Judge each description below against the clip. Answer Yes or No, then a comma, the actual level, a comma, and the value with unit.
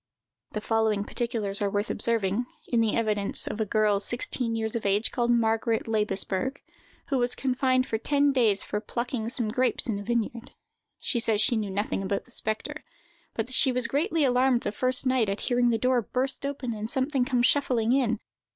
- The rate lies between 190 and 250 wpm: Yes, average, 195 wpm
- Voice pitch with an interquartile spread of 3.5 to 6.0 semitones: No, average, 3.0 semitones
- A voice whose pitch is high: Yes, high, 235 Hz